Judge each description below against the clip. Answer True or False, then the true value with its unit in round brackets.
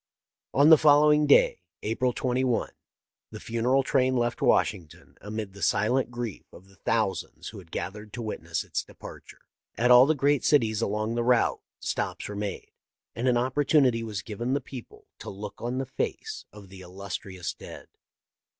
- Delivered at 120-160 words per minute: False (175 wpm)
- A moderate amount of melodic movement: True (4.0 semitones)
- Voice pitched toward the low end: True (120 Hz)